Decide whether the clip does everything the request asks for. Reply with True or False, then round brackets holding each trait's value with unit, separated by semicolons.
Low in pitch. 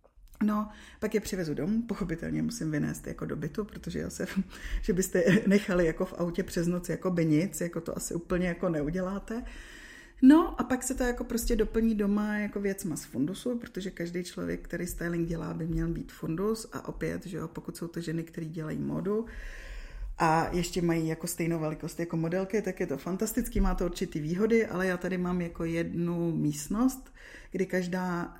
False (180 Hz)